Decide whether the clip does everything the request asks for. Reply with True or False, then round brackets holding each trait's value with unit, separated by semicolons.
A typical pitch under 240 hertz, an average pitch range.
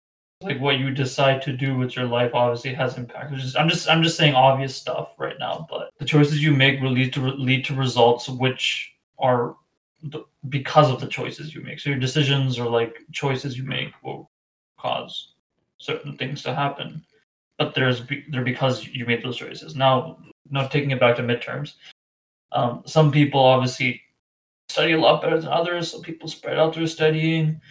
True (135 Hz; 3.1 semitones)